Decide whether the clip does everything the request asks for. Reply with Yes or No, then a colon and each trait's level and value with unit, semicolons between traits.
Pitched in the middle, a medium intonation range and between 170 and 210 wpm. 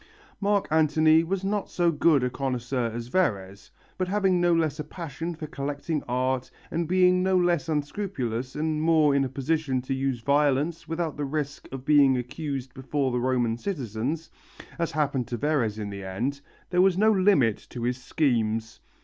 Yes: medium, 145 Hz; average, 4.7 semitones; average, 175 wpm